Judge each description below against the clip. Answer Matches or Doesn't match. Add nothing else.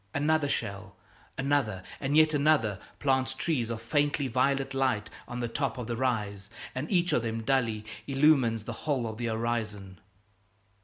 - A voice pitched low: Matches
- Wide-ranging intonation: Doesn't match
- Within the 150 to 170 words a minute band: Matches